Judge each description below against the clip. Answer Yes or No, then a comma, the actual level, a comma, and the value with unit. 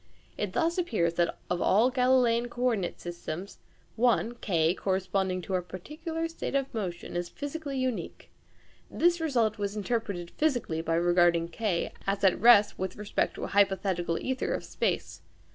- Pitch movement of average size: No, wide, 6.1 semitones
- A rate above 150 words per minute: Yes, average, 160 wpm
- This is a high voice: Yes, high, 205 Hz